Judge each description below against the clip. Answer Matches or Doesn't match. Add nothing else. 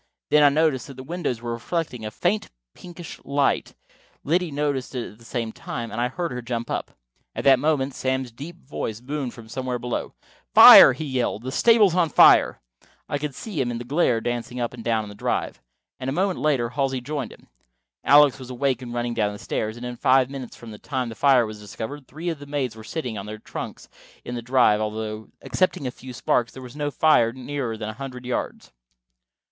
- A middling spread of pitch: Matches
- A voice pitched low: Matches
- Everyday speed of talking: Doesn't match